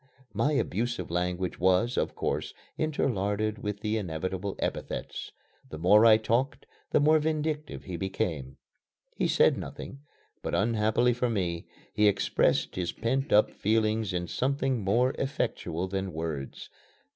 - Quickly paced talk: No, slow, 135 wpm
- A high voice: No, low, 105 Hz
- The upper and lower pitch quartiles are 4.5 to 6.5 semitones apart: Yes, average, 5.1 semitones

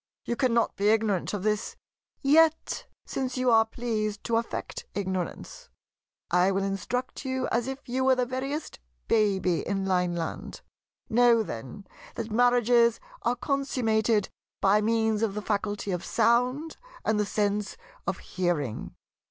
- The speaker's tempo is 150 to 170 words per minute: No, average, 140 wpm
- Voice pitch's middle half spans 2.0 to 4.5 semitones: Yes, average, 3.7 semitones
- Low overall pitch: No, high, 220 Hz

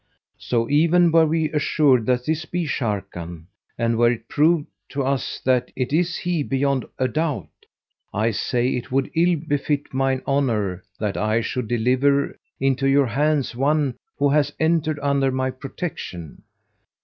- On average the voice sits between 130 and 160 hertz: Yes, low, 135 Hz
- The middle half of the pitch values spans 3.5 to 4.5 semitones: Yes, average, 3.8 semitones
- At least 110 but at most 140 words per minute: No, average, 155 wpm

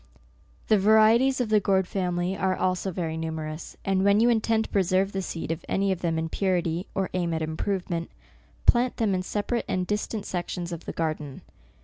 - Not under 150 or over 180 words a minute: No, average, 200 wpm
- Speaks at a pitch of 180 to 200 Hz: Yes, medium, 185 Hz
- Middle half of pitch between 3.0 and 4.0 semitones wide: Yes, average, 3.4 semitones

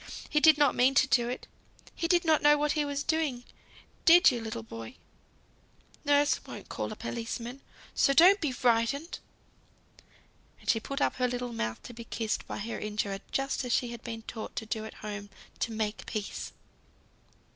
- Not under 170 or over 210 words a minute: Yes, average, 185 wpm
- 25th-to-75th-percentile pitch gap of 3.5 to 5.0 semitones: Yes, average, 4.6 semitones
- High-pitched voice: Yes, high, 245 Hz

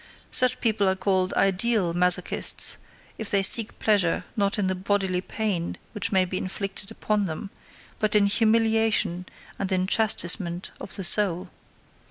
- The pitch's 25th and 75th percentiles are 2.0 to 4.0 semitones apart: Yes, narrow, 2.6 semitones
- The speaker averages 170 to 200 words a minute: No, average, 150 wpm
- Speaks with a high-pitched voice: Yes, high, 195 Hz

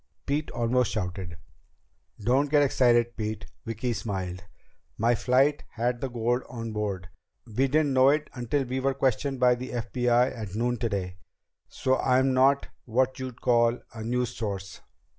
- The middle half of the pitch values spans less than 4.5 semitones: Yes, average, 2.9 semitones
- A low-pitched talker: Yes, low, 120 Hz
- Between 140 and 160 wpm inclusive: Yes, average, 155 wpm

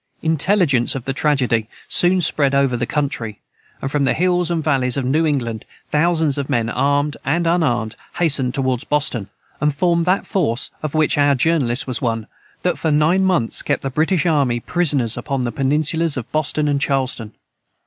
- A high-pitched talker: No, medium, 145 Hz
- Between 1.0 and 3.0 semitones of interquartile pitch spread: No, average, 4.1 semitones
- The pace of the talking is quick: No, average, 180 wpm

